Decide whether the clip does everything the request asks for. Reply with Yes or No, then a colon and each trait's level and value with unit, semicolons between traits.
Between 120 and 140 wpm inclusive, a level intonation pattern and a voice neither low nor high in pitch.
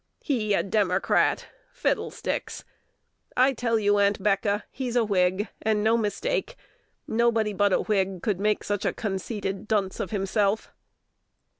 No: slow, 135 wpm; narrow, 2.1 semitones; high, 210 Hz